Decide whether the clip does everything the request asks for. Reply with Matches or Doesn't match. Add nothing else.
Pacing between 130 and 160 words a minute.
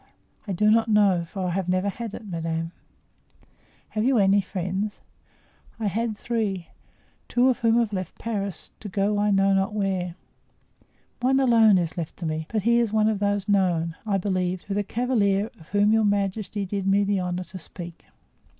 Doesn't match